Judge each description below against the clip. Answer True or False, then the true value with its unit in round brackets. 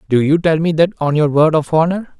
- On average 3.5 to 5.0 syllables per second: False (5.5 syllables/s)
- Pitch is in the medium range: True (160 Hz)